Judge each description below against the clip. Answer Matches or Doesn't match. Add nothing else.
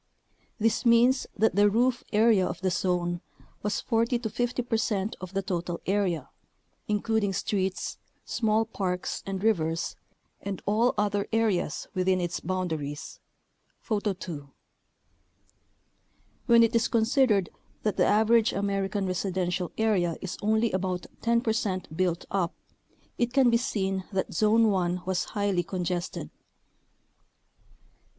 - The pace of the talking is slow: Matches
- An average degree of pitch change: Matches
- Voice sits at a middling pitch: Doesn't match